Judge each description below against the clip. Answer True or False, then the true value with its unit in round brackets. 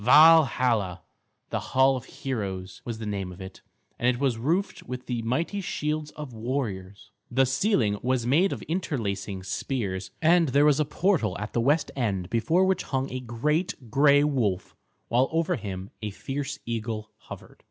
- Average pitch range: False (5.7 semitones)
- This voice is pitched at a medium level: False (125 Hz)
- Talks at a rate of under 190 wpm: True (170 wpm)